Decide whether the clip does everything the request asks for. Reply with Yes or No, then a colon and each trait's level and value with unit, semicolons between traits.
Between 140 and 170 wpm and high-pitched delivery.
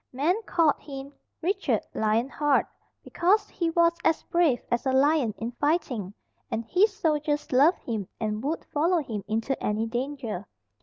Yes: average, 155 wpm; very high, 280 Hz